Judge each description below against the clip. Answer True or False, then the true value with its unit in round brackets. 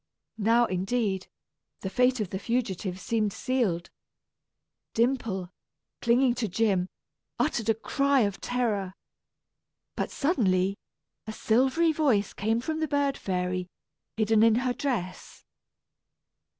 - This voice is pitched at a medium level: False (225 Hz)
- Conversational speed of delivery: False (115 wpm)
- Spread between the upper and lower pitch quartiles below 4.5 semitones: False (4.8 semitones)